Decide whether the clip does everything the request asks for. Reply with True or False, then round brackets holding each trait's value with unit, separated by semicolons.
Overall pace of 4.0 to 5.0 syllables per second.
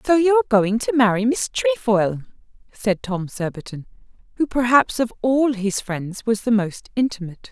True (4.7 syllables/s)